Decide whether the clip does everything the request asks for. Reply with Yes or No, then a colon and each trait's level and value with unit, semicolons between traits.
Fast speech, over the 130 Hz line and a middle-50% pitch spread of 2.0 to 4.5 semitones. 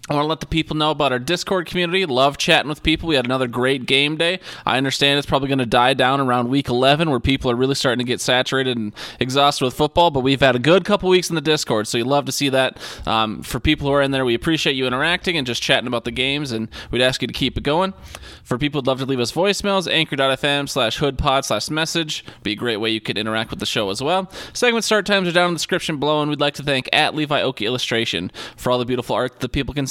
Yes: fast, 275 wpm; medium, 140 Hz; average, 3.9 semitones